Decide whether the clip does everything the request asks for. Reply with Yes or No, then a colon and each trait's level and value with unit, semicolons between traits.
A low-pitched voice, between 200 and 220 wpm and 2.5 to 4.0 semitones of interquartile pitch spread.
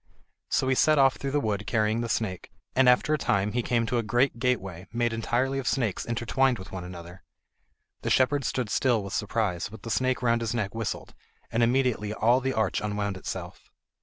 Yes: low, 115 Hz; fast, 205 wpm; average, 3.6 semitones